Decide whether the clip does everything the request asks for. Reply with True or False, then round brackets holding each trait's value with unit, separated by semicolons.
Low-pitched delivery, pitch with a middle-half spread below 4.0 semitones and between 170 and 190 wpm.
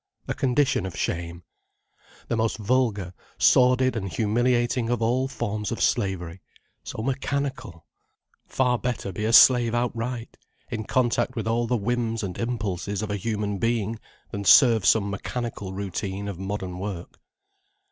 False (115 Hz; 3.5 semitones; 145 wpm)